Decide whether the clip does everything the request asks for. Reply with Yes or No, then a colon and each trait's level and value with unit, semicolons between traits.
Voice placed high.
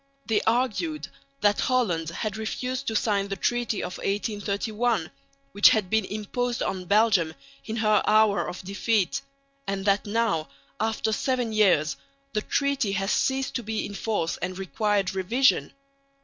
Yes: high, 210 Hz